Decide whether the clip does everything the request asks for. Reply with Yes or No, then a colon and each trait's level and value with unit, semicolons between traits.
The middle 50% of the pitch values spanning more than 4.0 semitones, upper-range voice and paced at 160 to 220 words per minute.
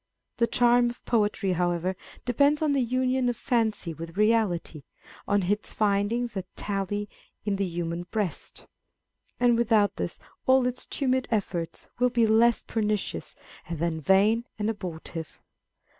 No: average, 4.4 semitones; high, 210 Hz; average, 140 wpm